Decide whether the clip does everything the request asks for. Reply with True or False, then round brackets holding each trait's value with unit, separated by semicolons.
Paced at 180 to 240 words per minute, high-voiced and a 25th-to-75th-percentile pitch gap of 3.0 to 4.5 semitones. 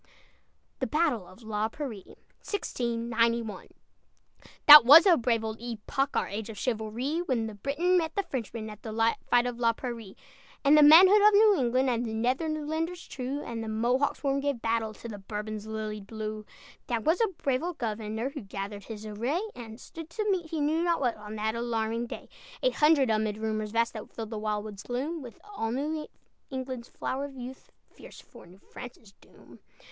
False (185 wpm; 235 Hz; 4.9 semitones)